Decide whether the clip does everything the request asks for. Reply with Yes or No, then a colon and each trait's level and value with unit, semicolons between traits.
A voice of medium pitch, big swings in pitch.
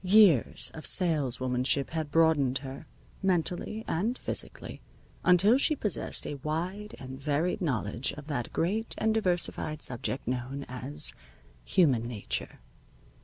Yes: medium, 155 Hz; wide, 5.9 semitones